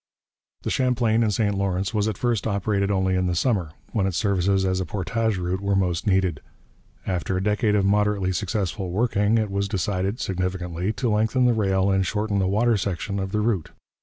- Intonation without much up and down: Yes, narrow, 2.3 semitones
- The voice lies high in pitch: No, low, 100 Hz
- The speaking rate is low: No, average, 195 wpm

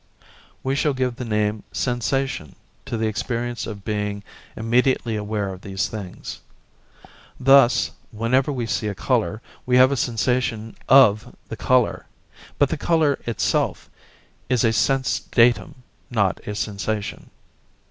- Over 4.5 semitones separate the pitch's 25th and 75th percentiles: No, average, 3.4 semitones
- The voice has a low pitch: Yes, low, 115 Hz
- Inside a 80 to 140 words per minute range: Yes, slow, 135 wpm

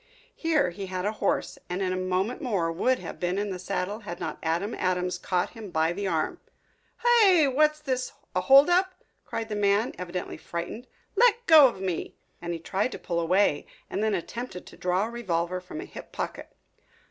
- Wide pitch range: Yes, wide, 6.0 semitones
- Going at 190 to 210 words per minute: Yes, average, 200 wpm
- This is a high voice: Yes, high, 200 Hz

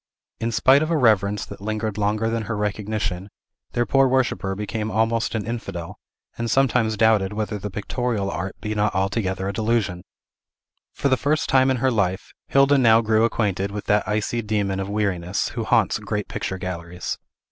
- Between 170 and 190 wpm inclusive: Yes, average, 180 wpm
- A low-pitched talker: Yes, low, 105 Hz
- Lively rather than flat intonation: No, average, 2.9 semitones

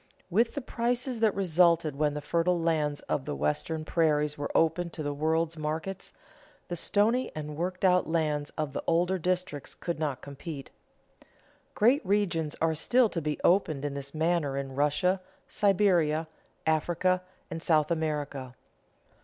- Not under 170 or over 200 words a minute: No, average, 155 wpm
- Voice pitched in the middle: Yes, medium, 160 Hz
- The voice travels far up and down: No, average, 3.4 semitones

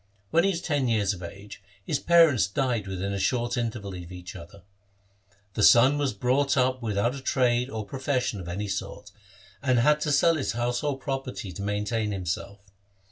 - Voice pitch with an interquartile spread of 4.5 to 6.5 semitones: Yes, average, 5.2 semitones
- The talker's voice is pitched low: Yes, low, 120 Hz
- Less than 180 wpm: No, average, 185 wpm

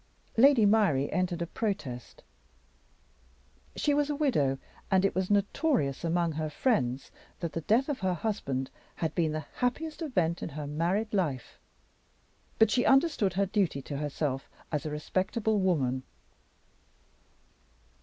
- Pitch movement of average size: No, wide, 6.8 semitones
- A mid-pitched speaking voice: Yes, medium, 180 Hz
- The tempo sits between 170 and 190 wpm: No, average, 140 wpm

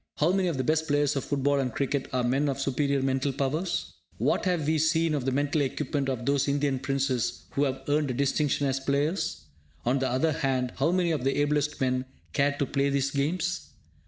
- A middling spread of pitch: No, narrow, 2.0 semitones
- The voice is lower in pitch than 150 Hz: Yes, medium, 140 Hz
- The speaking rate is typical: No, fast, 215 wpm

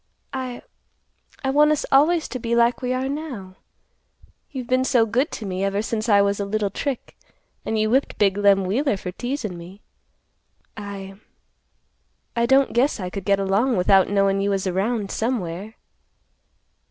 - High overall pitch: Yes, high, 215 Hz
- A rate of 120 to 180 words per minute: Yes, average, 160 wpm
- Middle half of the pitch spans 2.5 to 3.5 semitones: No, average, 4.6 semitones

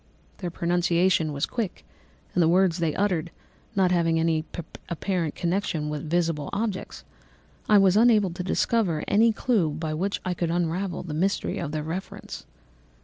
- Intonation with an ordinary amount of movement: Yes, average, 3.1 semitones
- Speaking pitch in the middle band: Yes, medium, 175 Hz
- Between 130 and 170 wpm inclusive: Yes, average, 155 wpm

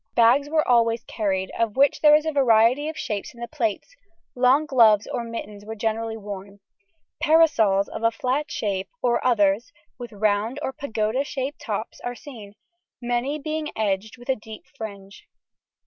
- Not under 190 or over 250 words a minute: No, average, 165 wpm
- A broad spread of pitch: No, average, 4.1 semitones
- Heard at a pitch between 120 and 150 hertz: No, high, 230 Hz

